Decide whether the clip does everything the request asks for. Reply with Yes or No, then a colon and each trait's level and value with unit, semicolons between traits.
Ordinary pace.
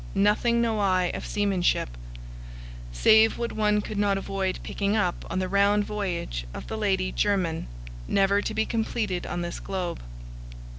Yes: average, 155 wpm